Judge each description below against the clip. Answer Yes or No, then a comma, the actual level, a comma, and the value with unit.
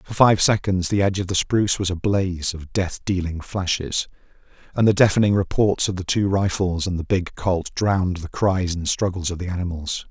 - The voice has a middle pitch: No, very low, 95 Hz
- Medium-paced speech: No, fast, 210 wpm